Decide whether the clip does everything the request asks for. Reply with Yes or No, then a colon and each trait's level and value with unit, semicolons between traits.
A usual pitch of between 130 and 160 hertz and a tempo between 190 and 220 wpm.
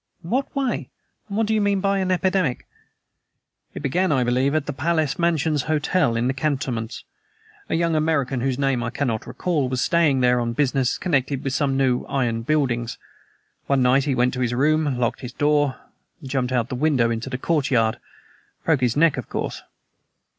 Yes: low, 135 Hz; average, 195 wpm